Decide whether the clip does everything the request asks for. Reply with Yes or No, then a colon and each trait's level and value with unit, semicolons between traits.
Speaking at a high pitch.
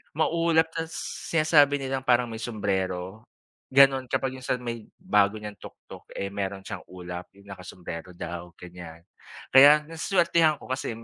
No: low, 120 Hz